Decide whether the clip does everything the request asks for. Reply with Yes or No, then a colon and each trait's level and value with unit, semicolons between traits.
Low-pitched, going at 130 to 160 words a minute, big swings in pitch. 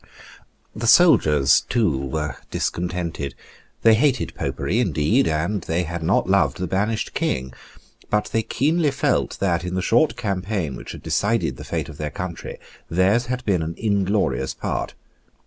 Yes: very low, 95 Hz; average, 155 wpm; wide, 5.9 semitones